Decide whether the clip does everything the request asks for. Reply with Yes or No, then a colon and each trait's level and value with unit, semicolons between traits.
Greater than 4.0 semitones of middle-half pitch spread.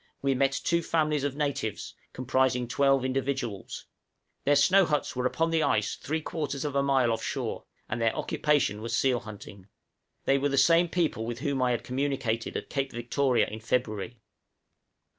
No: average, 3.2 semitones